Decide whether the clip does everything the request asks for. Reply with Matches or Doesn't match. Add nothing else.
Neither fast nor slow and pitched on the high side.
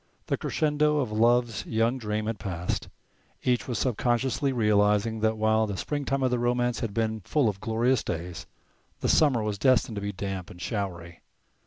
Doesn't match